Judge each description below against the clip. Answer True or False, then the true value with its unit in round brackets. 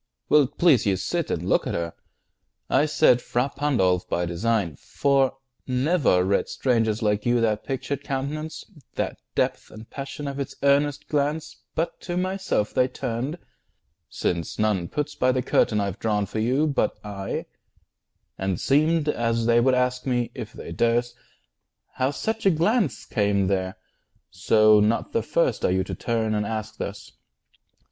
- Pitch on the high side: False (120 Hz)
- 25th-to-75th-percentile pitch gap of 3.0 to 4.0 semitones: False (5.1 semitones)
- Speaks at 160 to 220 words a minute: True (165 wpm)